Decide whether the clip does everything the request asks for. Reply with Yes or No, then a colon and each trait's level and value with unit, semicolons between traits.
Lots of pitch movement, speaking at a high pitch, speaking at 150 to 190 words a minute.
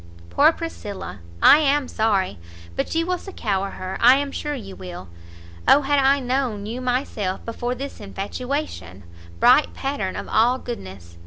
Yes: wide, 6.2 semitones; high, 245 Hz; average, 155 wpm